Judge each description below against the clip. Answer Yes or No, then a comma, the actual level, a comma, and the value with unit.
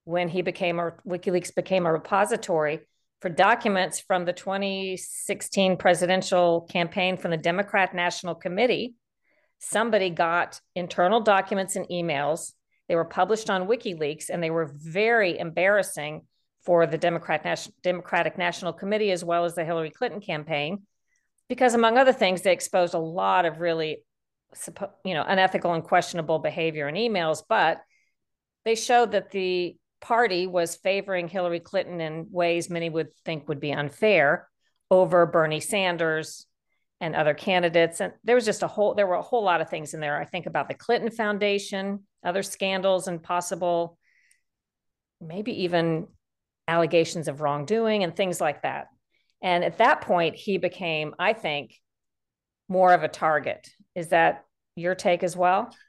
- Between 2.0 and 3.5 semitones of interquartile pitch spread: Yes, average, 2.9 semitones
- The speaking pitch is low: No, medium, 180 Hz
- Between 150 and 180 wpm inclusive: Yes, average, 155 wpm